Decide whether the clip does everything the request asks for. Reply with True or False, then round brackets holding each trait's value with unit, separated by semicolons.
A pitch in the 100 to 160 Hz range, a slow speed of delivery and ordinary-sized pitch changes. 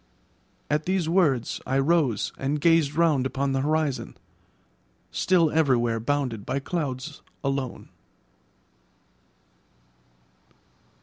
True (140 Hz; 90 wpm; 3.3 semitones)